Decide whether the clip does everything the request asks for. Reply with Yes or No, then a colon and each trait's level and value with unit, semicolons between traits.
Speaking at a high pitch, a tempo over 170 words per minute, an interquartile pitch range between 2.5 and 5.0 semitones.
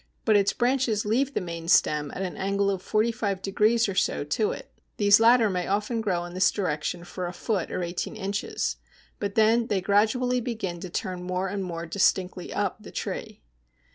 Yes: high, 200 Hz; average, 200 wpm; average, 3.4 semitones